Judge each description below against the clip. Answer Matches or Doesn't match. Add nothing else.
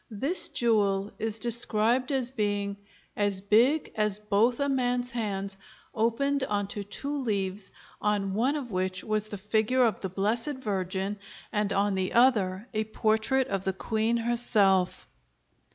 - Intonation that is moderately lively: Matches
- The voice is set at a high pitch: Matches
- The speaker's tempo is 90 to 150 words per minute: Matches